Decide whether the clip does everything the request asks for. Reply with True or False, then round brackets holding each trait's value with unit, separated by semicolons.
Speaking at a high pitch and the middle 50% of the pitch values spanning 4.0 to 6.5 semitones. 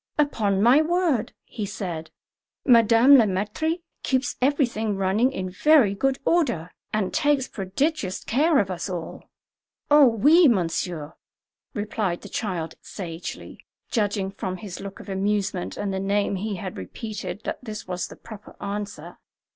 True (205 Hz; 5.3 semitones)